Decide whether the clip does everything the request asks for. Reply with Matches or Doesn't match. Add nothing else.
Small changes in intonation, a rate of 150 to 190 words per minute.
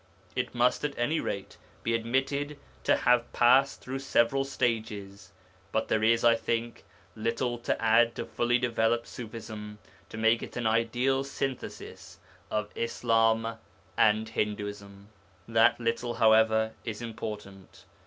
Doesn't match